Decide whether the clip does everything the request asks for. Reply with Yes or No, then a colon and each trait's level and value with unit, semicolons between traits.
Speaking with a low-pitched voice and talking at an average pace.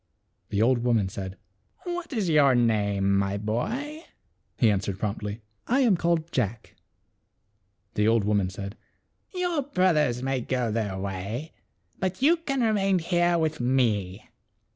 Yes: low, 125 Hz; average, 155 wpm